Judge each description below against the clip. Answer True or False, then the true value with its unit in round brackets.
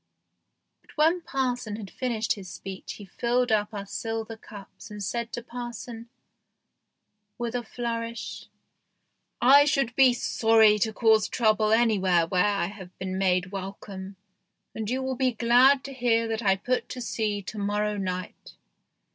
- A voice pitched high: True (225 Hz)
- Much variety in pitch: False (3.2 semitones)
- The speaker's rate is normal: True (155 wpm)